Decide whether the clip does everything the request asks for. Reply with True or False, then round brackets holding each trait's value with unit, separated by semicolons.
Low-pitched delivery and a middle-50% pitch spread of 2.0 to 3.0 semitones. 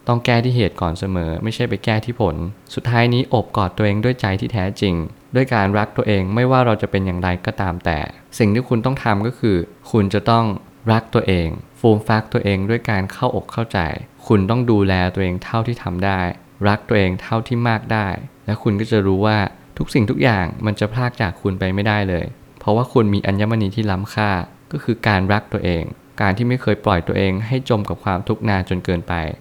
False (105 Hz; 3.5 semitones)